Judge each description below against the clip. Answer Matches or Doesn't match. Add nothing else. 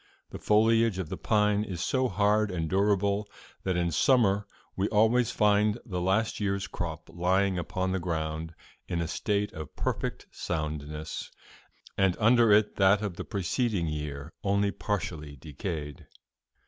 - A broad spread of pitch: Doesn't match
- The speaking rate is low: Doesn't match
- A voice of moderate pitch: Doesn't match